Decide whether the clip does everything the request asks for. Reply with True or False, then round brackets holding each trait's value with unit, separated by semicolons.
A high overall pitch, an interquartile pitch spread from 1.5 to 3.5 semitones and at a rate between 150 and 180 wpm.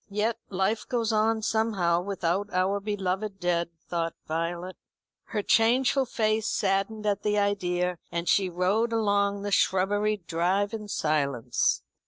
False (200 Hz; 3.2 semitones; 135 wpm)